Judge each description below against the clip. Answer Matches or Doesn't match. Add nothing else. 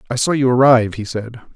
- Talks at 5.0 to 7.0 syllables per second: Matches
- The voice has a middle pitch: Doesn't match